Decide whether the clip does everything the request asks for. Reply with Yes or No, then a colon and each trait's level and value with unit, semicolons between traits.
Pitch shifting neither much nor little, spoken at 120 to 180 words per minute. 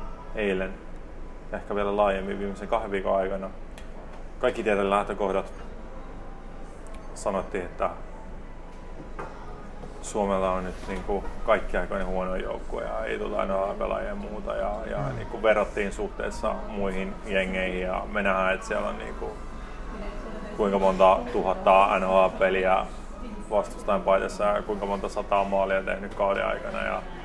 No: narrow, 1.3 semitones; average, 130 wpm